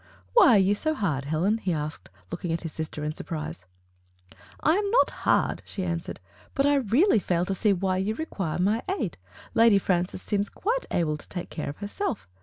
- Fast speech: Yes, fast, 210 wpm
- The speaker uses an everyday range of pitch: No, wide, 5.8 semitones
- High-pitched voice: Yes, high, 195 Hz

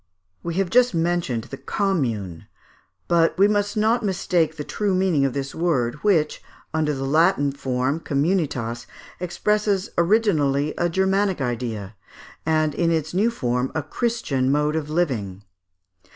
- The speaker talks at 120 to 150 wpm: Yes, average, 145 wpm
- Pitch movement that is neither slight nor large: No, wide, 5.9 semitones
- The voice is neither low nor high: Yes, medium, 160 Hz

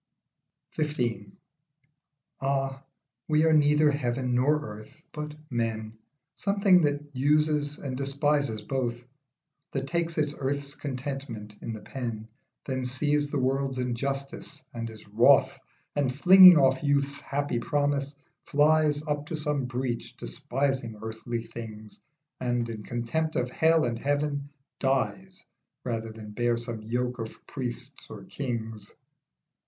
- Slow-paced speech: Yes, slow, 125 wpm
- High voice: No, low, 135 Hz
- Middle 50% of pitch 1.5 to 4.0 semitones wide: Yes, average, 3.7 semitones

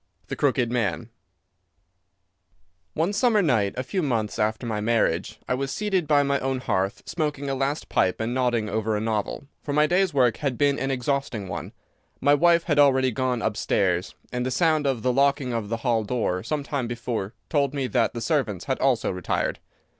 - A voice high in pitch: No, low, 130 Hz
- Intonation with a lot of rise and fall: No, average, 4.2 semitones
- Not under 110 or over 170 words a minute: No, average, 190 wpm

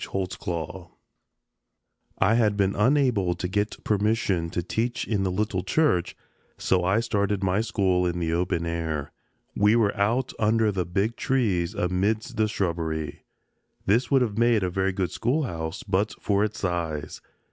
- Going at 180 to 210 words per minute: No, average, 155 wpm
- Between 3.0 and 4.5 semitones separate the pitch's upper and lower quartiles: Yes, average, 3.8 semitones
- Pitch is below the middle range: Yes, low, 100 Hz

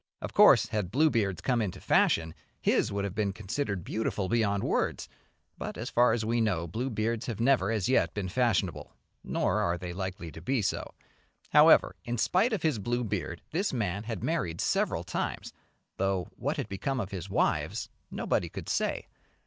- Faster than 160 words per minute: Yes, average, 185 wpm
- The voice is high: No, low, 105 Hz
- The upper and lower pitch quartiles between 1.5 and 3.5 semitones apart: No, average, 4.3 semitones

